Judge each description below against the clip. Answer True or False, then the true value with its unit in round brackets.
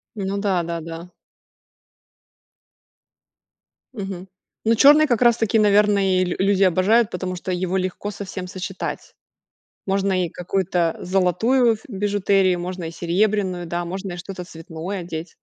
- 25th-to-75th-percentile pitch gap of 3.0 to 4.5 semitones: False (2.4 semitones)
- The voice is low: False (190 Hz)